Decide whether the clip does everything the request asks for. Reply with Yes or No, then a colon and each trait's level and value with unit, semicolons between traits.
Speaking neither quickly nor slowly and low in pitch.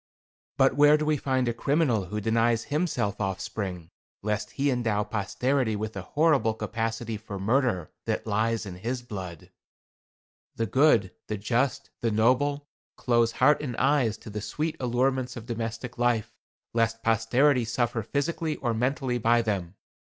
Yes: average, 150 wpm; low, 115 Hz